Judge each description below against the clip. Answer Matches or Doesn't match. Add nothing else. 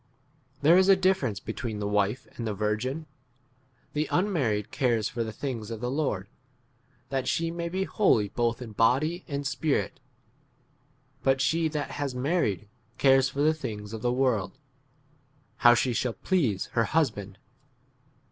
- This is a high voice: Doesn't match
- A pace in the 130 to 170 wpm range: Matches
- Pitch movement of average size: Doesn't match